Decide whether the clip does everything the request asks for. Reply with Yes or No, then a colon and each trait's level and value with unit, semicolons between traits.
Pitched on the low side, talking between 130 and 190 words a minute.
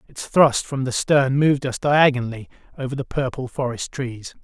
Yes: low, 130 Hz; average, 175 wpm